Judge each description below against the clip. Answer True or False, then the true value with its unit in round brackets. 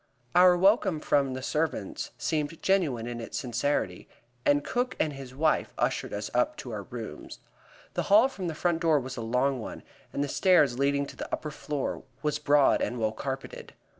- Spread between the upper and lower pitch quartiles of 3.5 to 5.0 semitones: True (4.6 semitones)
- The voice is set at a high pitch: False (140 Hz)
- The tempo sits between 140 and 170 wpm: False (190 wpm)